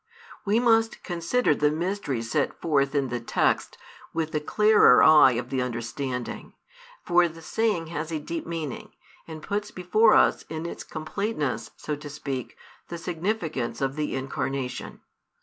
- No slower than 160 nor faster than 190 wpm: No, average, 150 wpm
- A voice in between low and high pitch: Yes, medium, 155 Hz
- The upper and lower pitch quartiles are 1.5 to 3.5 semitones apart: No, average, 4.6 semitones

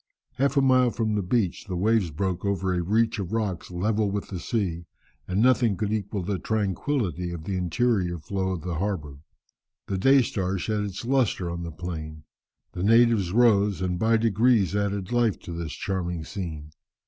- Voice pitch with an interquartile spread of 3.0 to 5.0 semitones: Yes, average, 4.0 semitones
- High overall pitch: No, low, 100 Hz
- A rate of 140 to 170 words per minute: No, average, 185 wpm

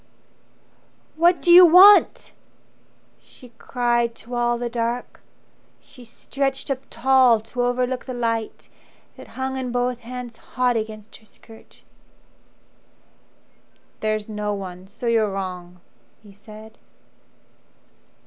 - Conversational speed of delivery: No, slow, 115 wpm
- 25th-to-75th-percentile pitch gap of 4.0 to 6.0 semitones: No, average, 2.7 semitones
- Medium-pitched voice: No, high, 240 Hz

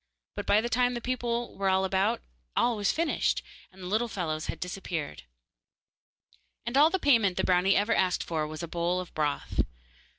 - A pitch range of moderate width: Yes, average, 5.0 semitones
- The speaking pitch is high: Yes, high, 195 Hz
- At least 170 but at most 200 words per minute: Yes, average, 185 wpm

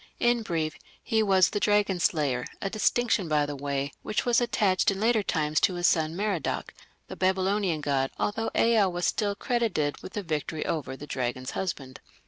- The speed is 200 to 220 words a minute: No, average, 180 wpm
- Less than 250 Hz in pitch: Yes, medium, 185 Hz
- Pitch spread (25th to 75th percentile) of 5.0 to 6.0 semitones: Yes, wide, 5.6 semitones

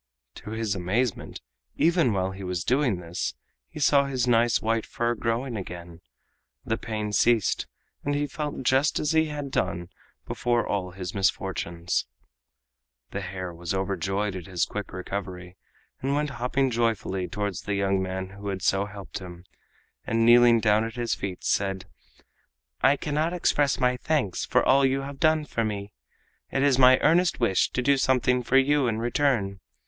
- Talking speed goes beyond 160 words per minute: Yes, average, 170 wpm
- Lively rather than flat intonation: Yes, wide, 5.7 semitones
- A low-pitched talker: Yes, low, 115 Hz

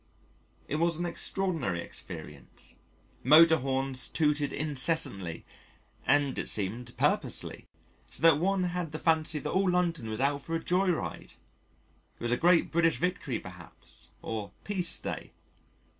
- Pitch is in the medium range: Yes, medium, 155 Hz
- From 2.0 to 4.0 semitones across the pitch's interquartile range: No, average, 4.8 semitones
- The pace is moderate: Yes, average, 145 wpm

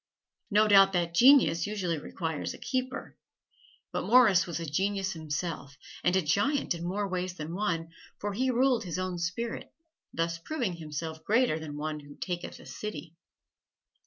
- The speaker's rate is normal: Yes, average, 160 wpm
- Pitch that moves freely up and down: No, average, 4.2 semitones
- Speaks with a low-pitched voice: No, medium, 180 Hz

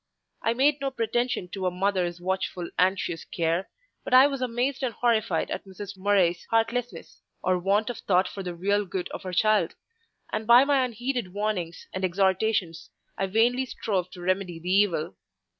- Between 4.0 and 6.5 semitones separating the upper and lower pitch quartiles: Yes, average, 4.4 semitones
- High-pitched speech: Yes, high, 200 Hz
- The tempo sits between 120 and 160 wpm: No, average, 175 wpm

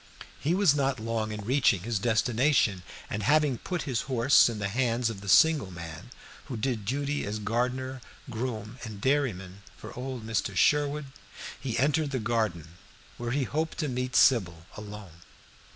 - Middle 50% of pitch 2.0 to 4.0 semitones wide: No, average, 4.4 semitones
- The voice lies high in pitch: No, low, 120 Hz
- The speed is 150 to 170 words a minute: Yes, average, 165 wpm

